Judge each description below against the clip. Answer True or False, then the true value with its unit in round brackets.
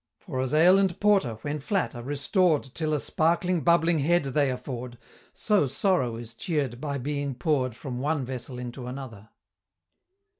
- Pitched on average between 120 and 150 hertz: True (140 Hz)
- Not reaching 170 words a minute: True (160 wpm)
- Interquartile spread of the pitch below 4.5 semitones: False (4.8 semitones)